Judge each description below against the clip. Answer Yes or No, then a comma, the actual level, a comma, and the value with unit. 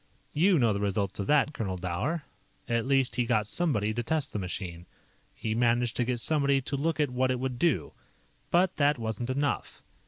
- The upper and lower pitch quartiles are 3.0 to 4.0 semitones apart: No, average, 4.9 semitones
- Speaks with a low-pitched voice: Yes, low, 125 Hz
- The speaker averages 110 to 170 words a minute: No, average, 195 wpm